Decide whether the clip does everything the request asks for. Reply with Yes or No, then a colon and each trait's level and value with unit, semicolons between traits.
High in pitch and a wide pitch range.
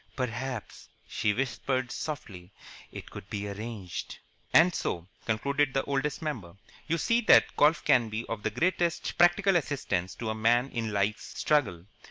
No: low, 120 Hz; wide, 6.0 semitones